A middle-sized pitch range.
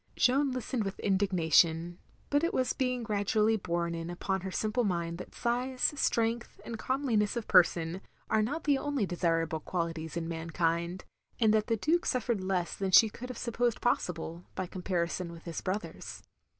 No: wide, 5.7 semitones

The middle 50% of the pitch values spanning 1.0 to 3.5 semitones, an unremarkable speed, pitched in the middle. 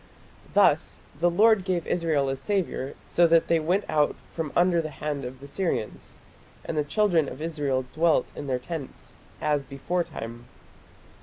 No: average, 4.0 semitones; average, 160 wpm; medium, 155 Hz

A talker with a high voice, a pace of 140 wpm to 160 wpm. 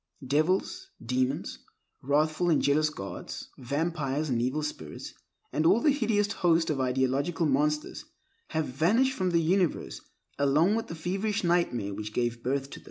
No: medium, 155 Hz; average, 155 wpm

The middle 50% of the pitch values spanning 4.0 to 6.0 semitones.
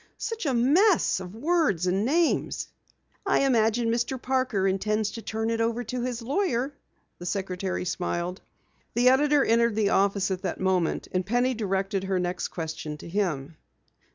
Yes: average, 5.1 semitones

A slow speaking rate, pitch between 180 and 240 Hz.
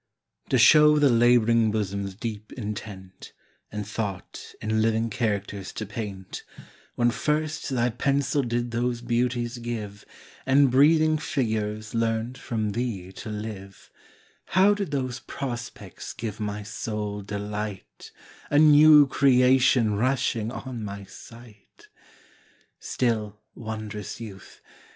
No: slow, 115 wpm; low, 115 Hz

